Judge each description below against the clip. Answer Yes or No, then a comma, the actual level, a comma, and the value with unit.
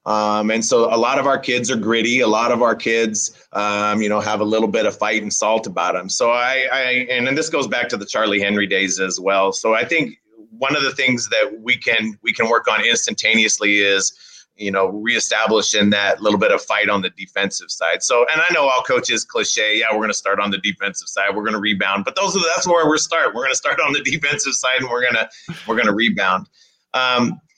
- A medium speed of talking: No, fast, 250 wpm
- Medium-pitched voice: No, low, 110 Hz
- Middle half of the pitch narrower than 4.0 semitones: Yes, average, 3.6 semitones